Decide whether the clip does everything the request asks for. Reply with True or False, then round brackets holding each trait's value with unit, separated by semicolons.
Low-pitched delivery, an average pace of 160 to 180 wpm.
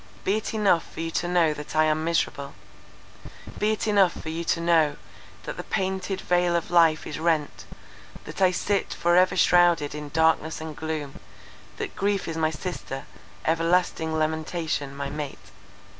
False (165 Hz; 165 wpm)